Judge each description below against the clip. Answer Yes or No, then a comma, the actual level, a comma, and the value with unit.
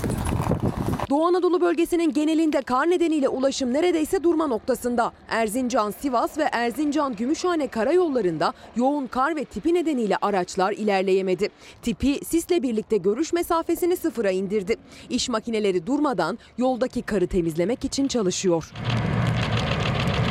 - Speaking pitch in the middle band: No, very high, 255 Hz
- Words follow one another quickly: No, average, 110 wpm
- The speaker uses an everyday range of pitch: No, wide, 6.8 semitones